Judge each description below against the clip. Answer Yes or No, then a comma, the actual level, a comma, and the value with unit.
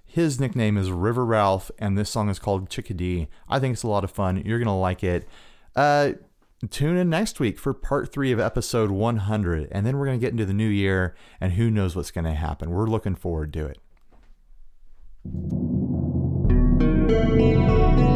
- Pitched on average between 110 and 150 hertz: No, low, 100 Hz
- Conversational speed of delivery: Yes, average, 185 wpm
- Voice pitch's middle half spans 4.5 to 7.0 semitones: Yes, average, 5.2 semitones